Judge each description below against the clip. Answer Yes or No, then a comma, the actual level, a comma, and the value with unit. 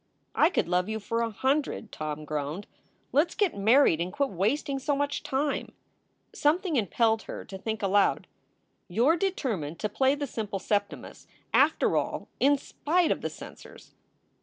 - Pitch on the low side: No, high, 230 Hz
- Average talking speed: Yes, average, 165 wpm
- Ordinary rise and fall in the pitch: No, wide, 6.6 semitones